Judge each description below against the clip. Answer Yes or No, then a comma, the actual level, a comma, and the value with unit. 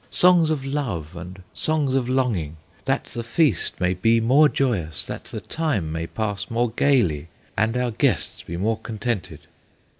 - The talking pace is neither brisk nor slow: Yes, average, 160 wpm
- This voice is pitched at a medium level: No, low, 115 Hz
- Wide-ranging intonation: Yes, wide, 6.8 semitones